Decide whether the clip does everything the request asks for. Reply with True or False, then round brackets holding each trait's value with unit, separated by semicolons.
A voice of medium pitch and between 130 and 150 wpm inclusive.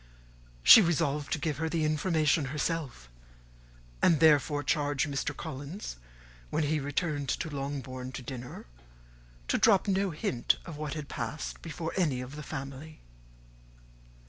True (150 Hz; 140 wpm)